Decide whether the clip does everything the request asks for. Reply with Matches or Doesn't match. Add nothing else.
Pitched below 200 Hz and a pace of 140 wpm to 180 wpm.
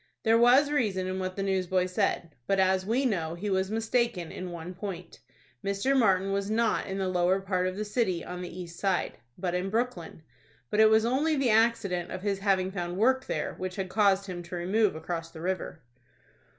Doesn't match